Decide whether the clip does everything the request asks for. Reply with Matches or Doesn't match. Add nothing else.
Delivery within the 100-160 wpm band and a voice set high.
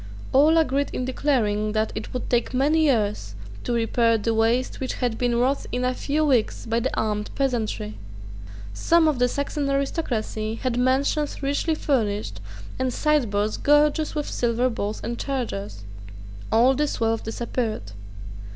Matches